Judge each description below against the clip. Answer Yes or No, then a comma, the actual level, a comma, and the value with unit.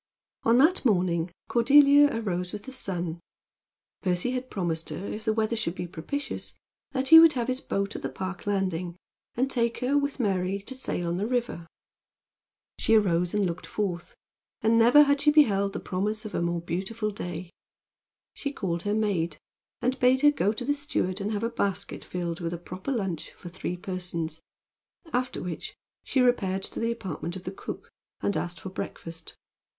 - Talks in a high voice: Yes, high, 200 Hz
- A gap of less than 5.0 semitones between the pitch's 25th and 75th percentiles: No, wide, 5.6 semitones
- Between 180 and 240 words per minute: Yes, average, 185 wpm